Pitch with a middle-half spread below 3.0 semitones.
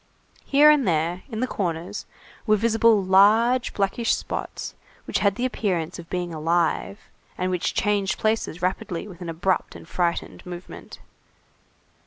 No: average, 4.0 semitones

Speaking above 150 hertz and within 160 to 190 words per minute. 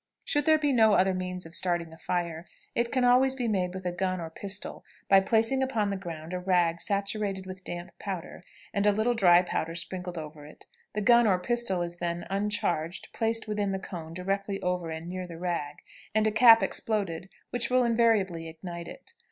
No: high, 190 Hz; average, 200 wpm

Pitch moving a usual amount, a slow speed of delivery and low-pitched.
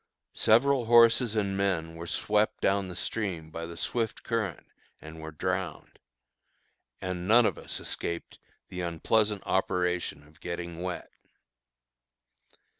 Yes: average, 4.2 semitones; slow, 125 wpm; very low, 95 Hz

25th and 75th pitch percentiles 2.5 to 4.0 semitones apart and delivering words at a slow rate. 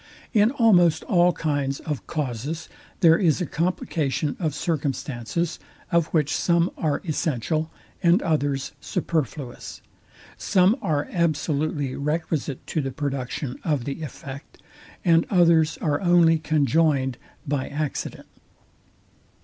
Yes: average, 3.1 semitones; slow, 115 wpm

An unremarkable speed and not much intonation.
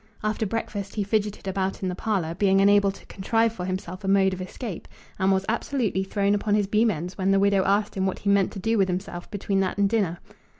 No: fast, 240 wpm; narrow, 1.7 semitones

